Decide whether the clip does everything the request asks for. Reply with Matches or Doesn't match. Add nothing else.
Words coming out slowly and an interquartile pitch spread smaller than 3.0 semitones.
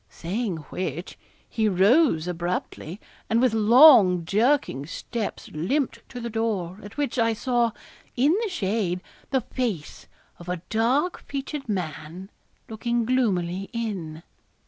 Doesn't match